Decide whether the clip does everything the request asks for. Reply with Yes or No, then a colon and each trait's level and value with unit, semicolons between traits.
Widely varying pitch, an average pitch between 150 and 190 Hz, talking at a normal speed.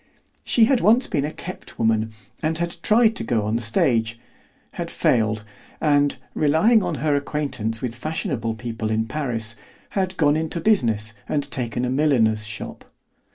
No: wide, 6.0 semitones; low, 135 Hz; average, 160 wpm